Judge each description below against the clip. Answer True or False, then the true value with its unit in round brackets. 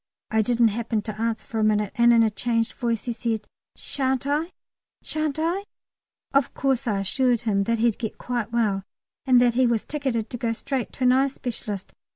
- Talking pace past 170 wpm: True (200 wpm)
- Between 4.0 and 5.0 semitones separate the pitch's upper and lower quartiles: False (2.8 semitones)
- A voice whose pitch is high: True (235 Hz)